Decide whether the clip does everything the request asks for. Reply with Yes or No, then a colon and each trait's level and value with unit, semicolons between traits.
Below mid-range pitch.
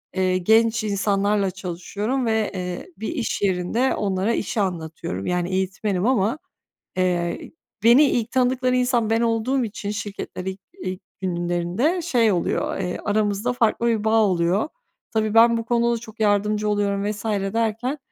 No: high, 210 Hz